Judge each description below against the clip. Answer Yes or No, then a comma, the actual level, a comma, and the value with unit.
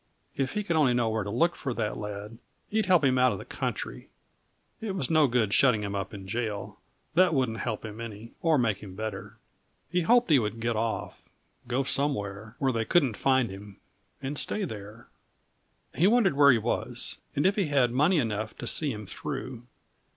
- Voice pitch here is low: Yes, low, 120 Hz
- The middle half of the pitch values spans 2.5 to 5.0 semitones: No, wide, 5.5 semitones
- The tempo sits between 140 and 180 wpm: No, average, 200 wpm